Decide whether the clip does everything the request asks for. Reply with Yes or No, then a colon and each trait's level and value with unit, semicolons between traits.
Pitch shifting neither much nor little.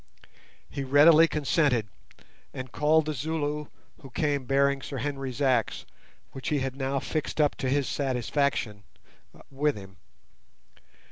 No: narrow, 2.3 semitones